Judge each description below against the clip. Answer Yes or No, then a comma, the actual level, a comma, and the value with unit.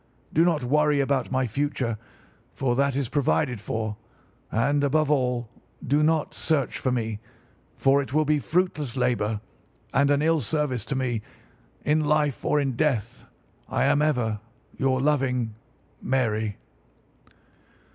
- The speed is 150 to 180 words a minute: No, average, 140 wpm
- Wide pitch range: No, average, 3.5 semitones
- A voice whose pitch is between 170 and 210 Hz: No, low, 135 Hz